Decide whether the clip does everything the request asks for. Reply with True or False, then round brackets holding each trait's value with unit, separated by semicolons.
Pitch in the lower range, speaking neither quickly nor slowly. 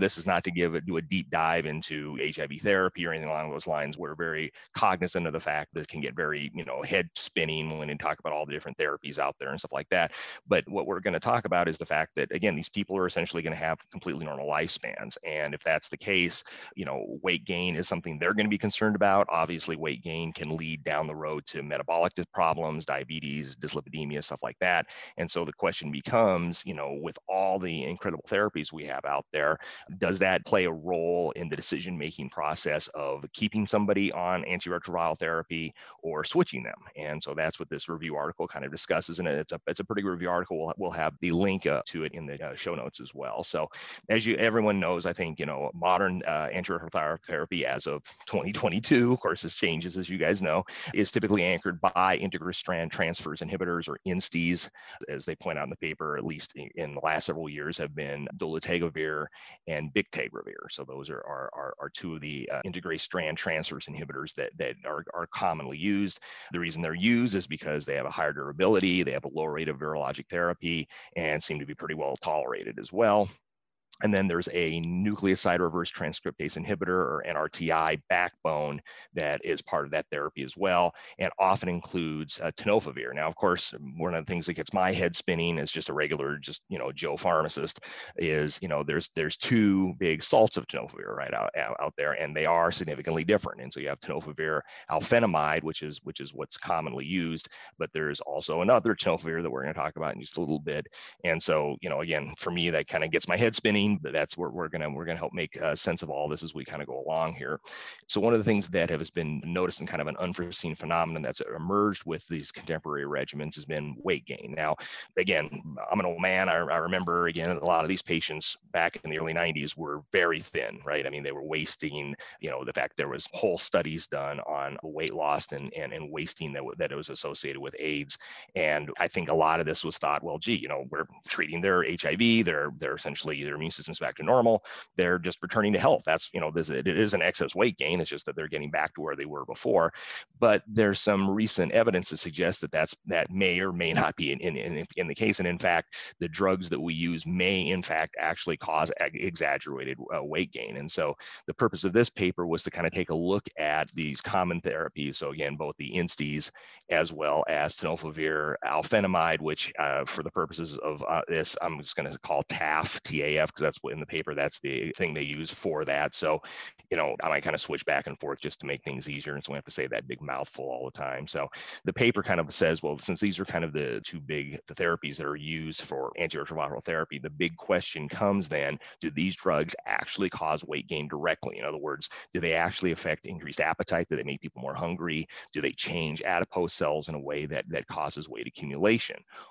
False (85 Hz; 225 wpm)